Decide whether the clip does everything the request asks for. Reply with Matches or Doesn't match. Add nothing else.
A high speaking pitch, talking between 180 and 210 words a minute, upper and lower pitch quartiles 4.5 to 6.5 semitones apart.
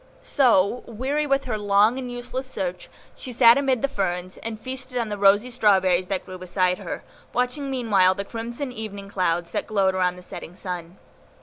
Matches